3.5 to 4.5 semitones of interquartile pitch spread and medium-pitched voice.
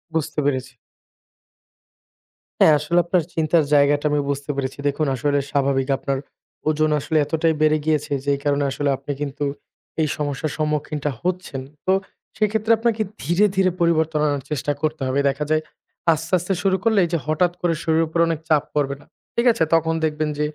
No: narrow, 2.5 semitones; medium, 155 Hz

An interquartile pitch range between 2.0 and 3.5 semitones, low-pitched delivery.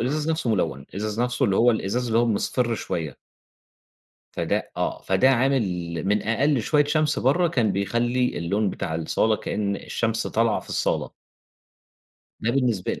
No: average, 3.9 semitones; low, 115 Hz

